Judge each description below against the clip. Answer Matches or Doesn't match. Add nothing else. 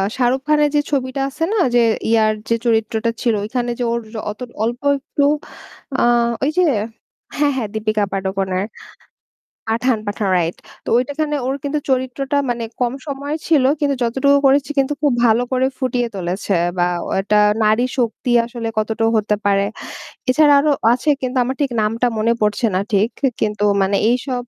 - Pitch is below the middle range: Doesn't match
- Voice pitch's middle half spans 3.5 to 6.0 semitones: Matches